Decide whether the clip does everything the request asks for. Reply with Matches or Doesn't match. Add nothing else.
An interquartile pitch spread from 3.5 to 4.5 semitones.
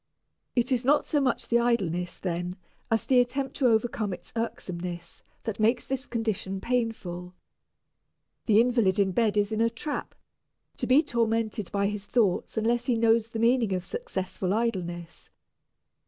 Matches